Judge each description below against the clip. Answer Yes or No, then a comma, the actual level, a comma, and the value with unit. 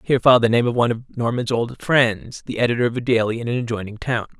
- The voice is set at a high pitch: No, low, 120 Hz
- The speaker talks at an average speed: No, fast, 260 wpm